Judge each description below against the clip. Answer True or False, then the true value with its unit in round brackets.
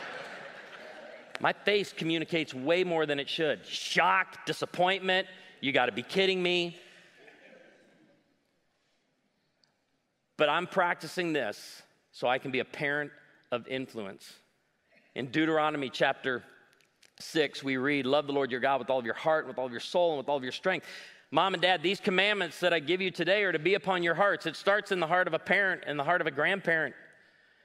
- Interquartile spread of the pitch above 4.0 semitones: True (4.7 semitones)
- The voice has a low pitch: False (165 Hz)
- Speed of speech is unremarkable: True (180 wpm)